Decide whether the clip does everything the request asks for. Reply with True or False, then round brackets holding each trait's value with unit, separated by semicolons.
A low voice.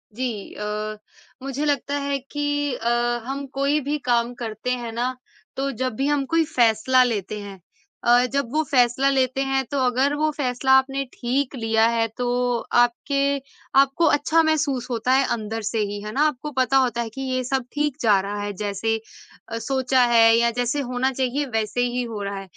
False (250 Hz)